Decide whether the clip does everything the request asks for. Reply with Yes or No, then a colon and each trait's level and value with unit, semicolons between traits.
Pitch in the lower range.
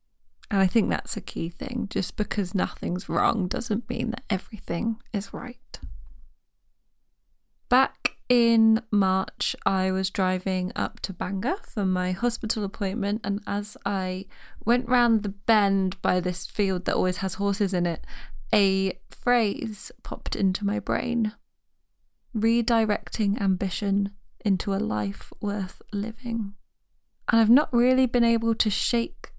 No: high, 205 Hz